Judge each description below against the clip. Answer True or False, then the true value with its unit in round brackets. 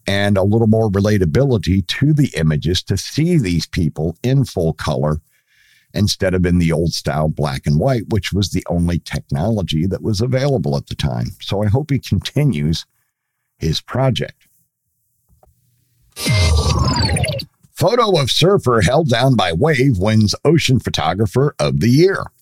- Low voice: True (105 Hz)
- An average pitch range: False (7.1 semitones)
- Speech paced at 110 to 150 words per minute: True (145 wpm)